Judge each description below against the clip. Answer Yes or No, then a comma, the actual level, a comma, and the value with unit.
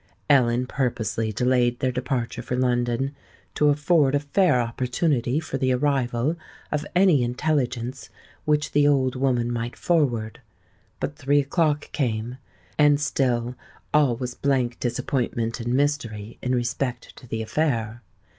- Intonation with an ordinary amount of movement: Yes, average, 3.2 semitones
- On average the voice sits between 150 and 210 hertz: No, low, 125 Hz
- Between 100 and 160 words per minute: Yes, slow, 135 wpm